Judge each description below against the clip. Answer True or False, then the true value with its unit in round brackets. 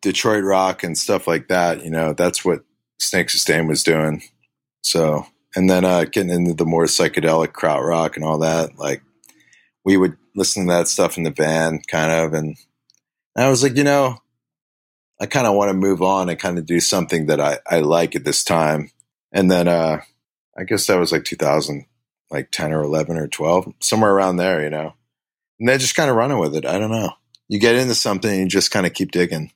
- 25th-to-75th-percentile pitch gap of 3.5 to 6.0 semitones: True (3.9 semitones)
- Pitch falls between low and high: False (90 Hz)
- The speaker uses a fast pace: True (215 wpm)